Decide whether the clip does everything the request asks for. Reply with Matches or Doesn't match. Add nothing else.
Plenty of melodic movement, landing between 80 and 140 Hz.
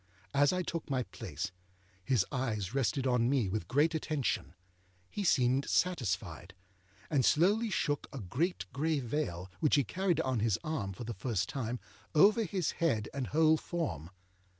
Matches